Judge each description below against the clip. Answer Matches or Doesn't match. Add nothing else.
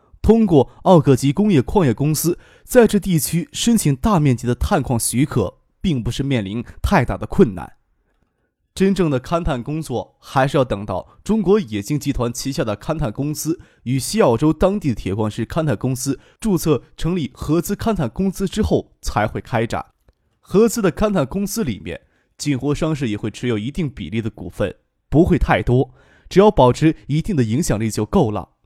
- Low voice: Doesn't match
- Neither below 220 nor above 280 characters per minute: Matches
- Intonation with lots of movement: Matches